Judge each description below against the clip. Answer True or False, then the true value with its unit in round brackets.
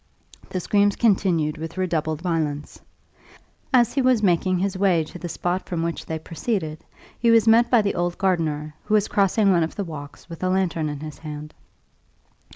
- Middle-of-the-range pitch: True (175 Hz)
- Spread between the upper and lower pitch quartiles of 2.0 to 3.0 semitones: False (4.1 semitones)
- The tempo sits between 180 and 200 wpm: True (185 wpm)